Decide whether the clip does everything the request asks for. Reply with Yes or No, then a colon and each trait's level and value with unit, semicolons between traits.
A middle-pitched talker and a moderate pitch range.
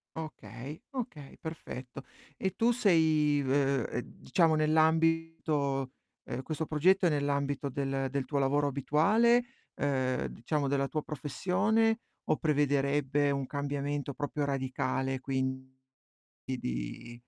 Yes: medium, 145 Hz; average, 3.0 semitones